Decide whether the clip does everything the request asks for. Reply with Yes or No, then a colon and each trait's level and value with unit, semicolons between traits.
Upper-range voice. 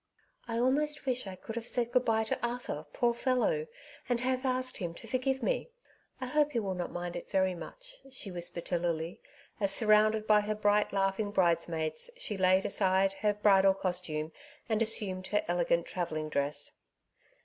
Yes: high, 205 Hz